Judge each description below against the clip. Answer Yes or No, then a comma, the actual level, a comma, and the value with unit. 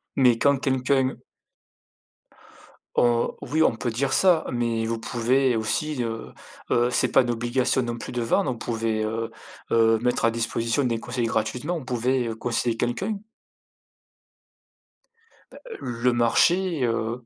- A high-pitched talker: No, low, 120 Hz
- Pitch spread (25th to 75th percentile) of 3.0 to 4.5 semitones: No, narrow, 2.4 semitones